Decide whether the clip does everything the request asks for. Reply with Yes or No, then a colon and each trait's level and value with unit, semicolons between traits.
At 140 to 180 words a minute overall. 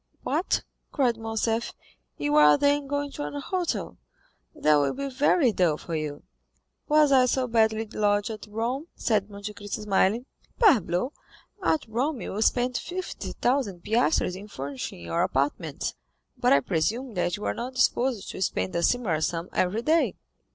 Yes: average, 160 wpm